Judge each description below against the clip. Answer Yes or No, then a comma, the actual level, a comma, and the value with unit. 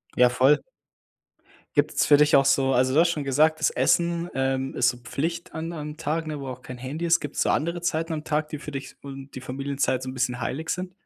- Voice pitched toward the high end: No, medium, 145 Hz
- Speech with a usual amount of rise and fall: Yes, average, 3.3 semitones